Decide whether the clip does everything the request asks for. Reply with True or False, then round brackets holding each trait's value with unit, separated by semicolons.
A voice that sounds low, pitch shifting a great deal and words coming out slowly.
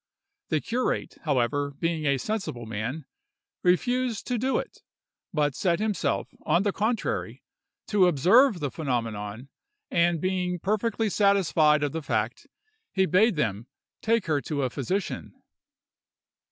False (170 Hz; 6.5 semitones; 130 wpm)